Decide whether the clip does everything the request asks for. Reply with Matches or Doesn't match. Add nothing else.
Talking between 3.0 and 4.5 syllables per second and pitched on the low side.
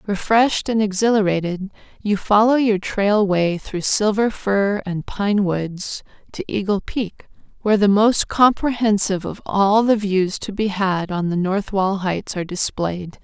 Doesn't match